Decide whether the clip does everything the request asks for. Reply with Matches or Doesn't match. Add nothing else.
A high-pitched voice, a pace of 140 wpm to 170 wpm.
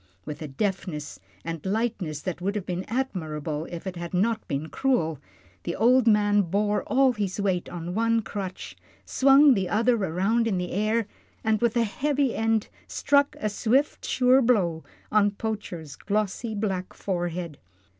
Matches